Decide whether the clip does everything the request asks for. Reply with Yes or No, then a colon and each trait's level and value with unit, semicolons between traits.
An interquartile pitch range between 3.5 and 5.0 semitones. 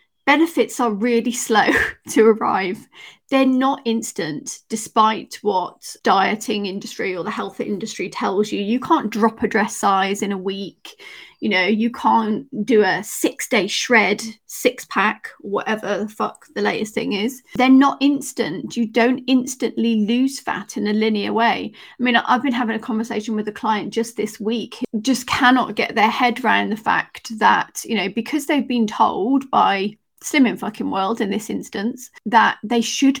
No: average, 2.7 semitones